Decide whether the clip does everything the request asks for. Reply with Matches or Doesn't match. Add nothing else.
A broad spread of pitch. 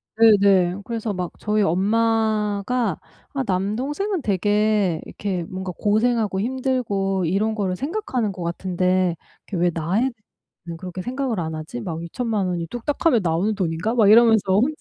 Doesn't match